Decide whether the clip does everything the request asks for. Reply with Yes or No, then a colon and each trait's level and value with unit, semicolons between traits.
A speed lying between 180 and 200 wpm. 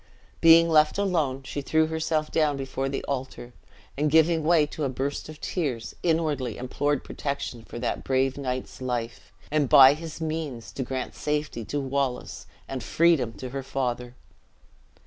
No: average, 160 wpm